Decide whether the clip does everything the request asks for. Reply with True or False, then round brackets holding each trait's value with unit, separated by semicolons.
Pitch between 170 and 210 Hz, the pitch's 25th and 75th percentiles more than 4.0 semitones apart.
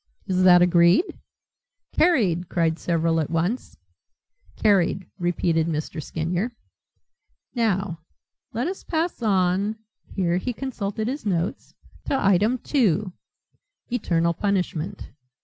True (185 Hz; 4.4 semitones)